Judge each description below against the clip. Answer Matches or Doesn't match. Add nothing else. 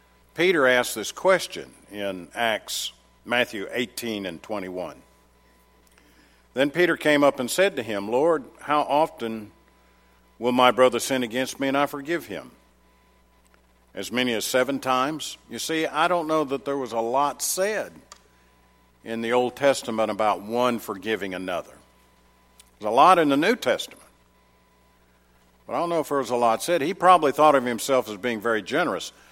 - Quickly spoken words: Doesn't match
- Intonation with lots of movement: Matches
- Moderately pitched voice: Doesn't match